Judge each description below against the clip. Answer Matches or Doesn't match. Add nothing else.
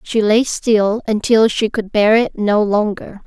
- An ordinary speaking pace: Matches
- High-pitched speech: Matches